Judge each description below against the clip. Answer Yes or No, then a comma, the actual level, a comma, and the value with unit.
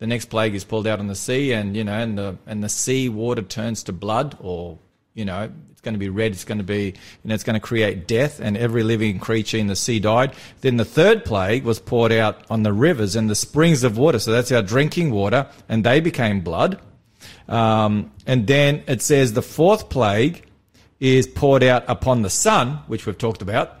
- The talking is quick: Yes, fast, 230 wpm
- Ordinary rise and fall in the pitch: Yes, average, 3.5 semitones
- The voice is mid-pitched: No, low, 115 Hz